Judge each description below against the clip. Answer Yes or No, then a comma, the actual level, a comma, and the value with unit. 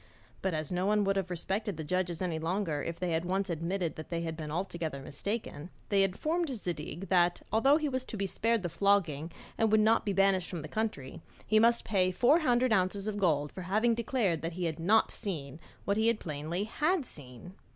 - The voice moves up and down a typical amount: Yes, average, 4.6 semitones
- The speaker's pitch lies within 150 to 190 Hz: Yes, medium, 185 Hz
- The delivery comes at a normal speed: No, fast, 210 wpm